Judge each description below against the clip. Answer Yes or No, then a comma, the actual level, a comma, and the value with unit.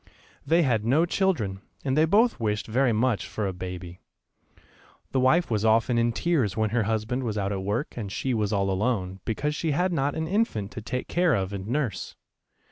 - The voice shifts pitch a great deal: Yes, wide, 6.1 semitones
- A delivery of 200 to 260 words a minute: Yes, fast, 205 wpm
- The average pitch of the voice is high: No, low, 115 Hz